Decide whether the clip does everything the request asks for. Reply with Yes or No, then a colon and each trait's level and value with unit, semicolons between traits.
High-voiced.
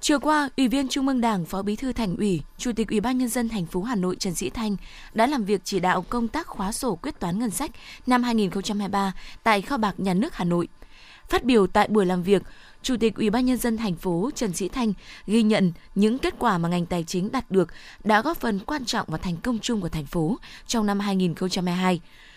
Yes: high, 210 Hz